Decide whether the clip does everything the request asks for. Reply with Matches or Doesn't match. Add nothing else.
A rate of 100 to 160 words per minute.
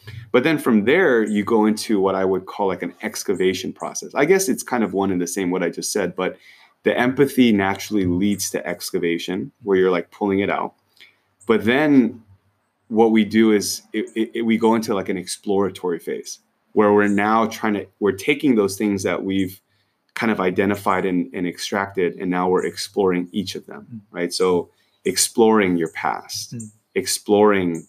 Doesn't match